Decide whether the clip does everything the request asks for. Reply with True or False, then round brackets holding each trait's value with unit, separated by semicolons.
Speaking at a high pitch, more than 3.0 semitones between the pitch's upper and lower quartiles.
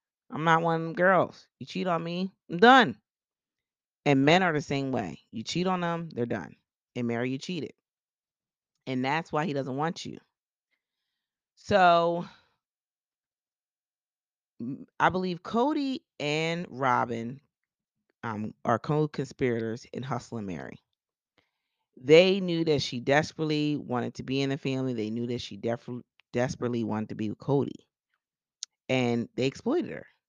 False (140 Hz; 5.5 semitones)